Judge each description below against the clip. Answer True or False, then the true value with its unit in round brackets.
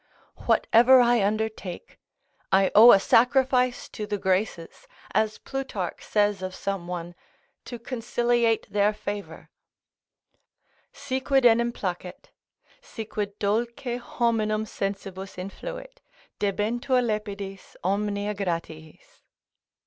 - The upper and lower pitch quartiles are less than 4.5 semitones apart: True (3.5 semitones)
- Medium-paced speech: False (105 wpm)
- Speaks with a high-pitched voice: True (210 Hz)